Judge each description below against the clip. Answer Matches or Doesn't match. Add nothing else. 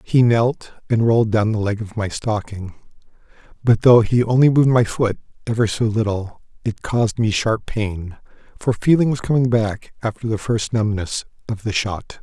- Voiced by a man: Matches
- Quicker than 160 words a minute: Matches